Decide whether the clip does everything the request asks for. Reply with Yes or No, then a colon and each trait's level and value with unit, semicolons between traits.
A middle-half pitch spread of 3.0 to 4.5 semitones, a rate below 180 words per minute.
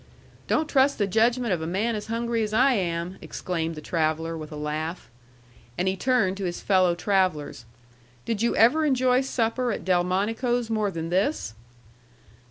No: wide, 5.5 semitones; average, 170 wpm